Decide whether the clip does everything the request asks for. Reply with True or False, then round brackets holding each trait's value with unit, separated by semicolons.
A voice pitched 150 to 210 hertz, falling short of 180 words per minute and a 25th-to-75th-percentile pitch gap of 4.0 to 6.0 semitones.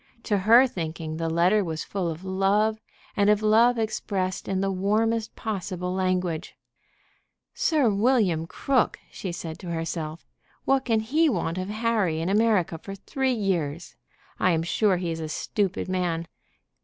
True (190 Hz; 155 wpm; 4.4 semitones)